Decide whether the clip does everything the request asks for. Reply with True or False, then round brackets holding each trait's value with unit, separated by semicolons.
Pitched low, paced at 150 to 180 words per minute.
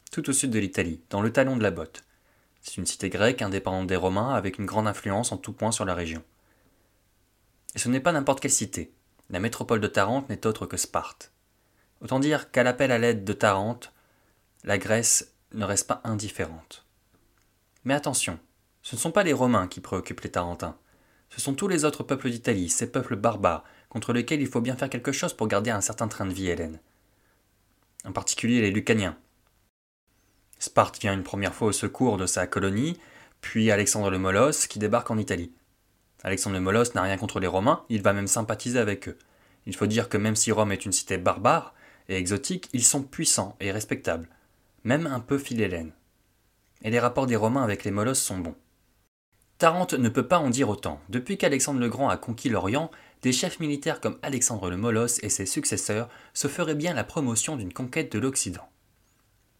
False (110 Hz; 195 wpm)